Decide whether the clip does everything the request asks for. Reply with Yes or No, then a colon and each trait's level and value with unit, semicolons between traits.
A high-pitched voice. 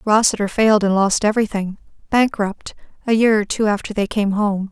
Yes: high, 210 Hz